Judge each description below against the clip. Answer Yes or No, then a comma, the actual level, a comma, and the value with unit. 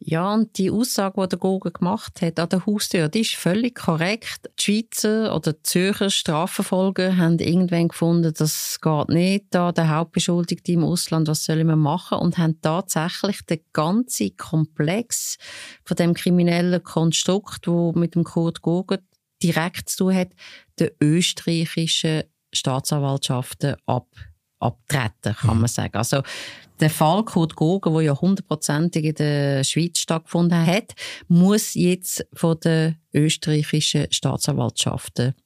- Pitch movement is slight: No, average, 3.2 semitones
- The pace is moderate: Yes, average, 140 wpm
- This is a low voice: No, medium, 165 Hz